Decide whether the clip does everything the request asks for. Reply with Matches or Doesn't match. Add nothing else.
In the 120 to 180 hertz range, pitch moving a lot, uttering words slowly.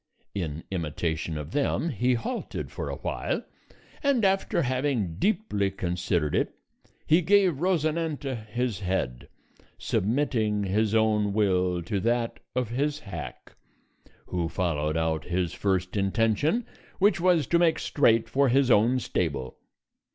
Doesn't match